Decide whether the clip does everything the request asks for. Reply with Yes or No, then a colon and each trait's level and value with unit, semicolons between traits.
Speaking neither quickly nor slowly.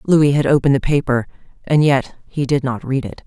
No: fast, 220 wpm